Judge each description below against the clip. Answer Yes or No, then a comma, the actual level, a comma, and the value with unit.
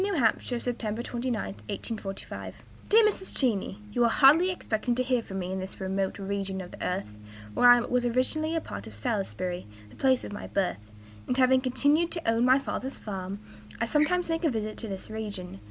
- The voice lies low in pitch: No, high, 230 Hz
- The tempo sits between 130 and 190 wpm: No, average, 200 wpm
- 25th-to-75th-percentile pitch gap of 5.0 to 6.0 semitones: Yes, wide, 5.4 semitones